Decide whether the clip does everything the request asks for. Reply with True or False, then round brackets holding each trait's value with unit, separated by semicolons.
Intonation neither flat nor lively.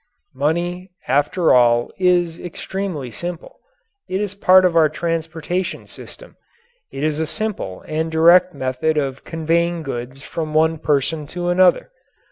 True (3.3 semitones)